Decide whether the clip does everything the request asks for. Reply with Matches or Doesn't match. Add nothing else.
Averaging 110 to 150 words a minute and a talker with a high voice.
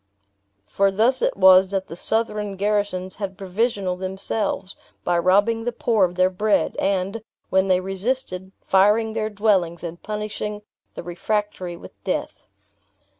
Matches